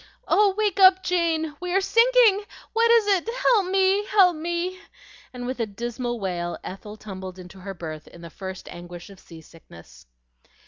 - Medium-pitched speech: No, very high, 255 Hz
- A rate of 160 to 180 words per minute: Yes, average, 170 wpm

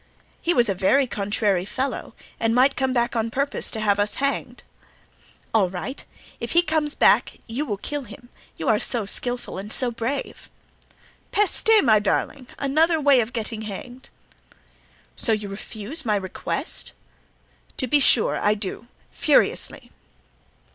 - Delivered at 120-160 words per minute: Yes, average, 150 wpm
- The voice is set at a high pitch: Yes, high, 235 Hz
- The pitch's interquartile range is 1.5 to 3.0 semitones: No, average, 4.7 semitones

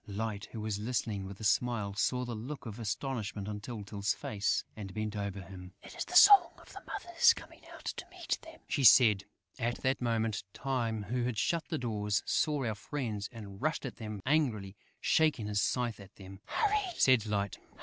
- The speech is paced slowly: No, average, 195 wpm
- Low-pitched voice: Yes, low, 110 Hz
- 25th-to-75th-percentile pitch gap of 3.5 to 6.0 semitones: Yes, average, 4.2 semitones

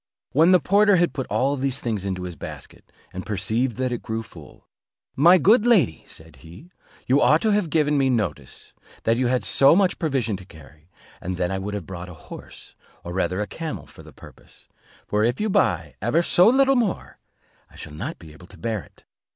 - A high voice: No, low, 120 Hz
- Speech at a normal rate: No, fast, 210 wpm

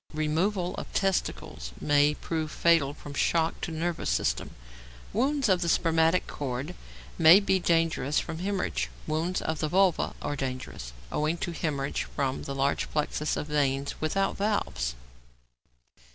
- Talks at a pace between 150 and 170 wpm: No, average, 140 wpm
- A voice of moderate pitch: Yes, medium, 155 Hz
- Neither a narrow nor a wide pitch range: Yes, average, 3.7 semitones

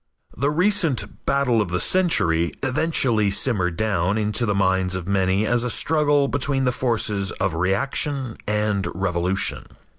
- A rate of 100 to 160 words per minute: Yes, average, 145 wpm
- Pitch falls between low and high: No, low, 105 Hz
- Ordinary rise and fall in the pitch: No, wide, 6.3 semitones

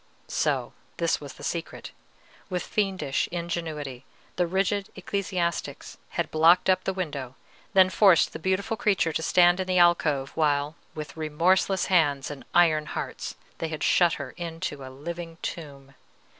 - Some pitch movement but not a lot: Yes, average, 3.6 semitones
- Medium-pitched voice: Yes, medium, 170 Hz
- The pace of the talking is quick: No, average, 150 wpm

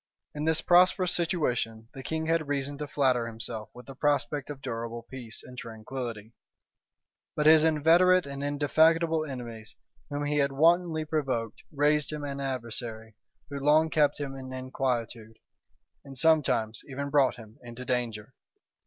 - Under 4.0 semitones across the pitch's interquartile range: No, average, 4.3 semitones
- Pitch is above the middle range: No, medium, 140 Hz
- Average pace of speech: Yes, average, 150 wpm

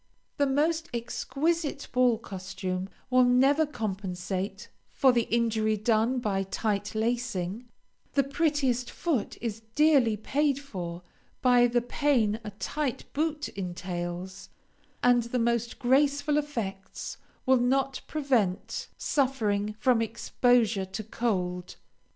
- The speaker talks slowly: Yes, slow, 115 wpm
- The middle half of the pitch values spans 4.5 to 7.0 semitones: Yes, average, 5.2 semitones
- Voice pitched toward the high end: Yes, high, 235 Hz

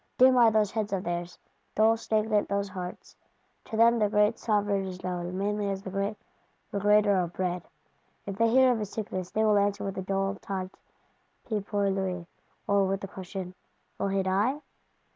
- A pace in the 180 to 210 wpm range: Yes, average, 185 wpm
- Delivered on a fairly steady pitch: Yes, narrow, 2.0 semitones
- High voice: Yes, high, 200 Hz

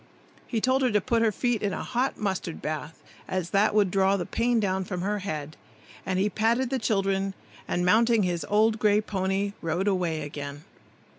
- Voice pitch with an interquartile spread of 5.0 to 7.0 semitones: No, average, 3.2 semitones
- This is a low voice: No, high, 195 Hz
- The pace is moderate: Yes, average, 195 wpm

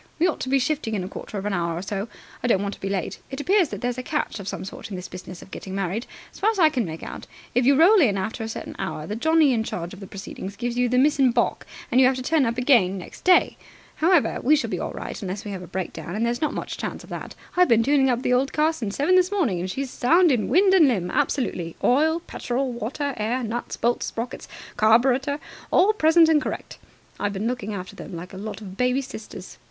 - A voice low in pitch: No, high, 245 Hz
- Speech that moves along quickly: Yes, fast, 265 wpm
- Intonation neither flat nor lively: No, wide, 6.4 semitones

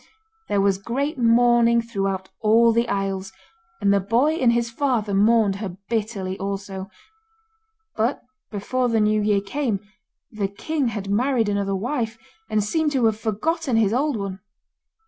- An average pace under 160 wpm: Yes, average, 150 wpm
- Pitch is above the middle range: Yes, high, 220 Hz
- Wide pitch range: No, average, 3.2 semitones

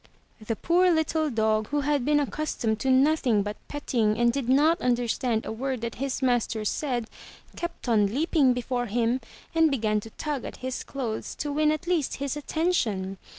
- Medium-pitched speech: No, very high, 255 Hz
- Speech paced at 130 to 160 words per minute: No, average, 185 wpm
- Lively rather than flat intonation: No, average, 4.7 semitones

